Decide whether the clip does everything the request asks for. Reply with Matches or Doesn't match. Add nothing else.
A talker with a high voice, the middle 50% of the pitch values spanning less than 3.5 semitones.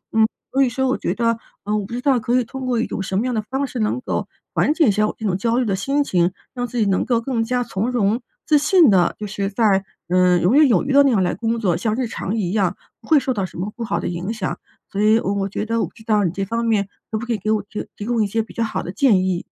Doesn't match